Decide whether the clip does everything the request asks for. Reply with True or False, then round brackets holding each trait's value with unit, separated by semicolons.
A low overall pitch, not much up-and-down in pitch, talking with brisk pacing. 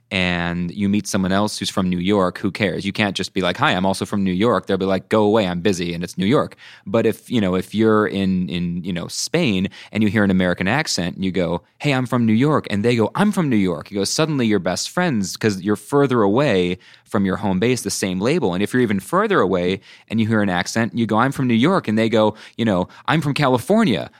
False (100 Hz; 3.4 semitones; 270 wpm)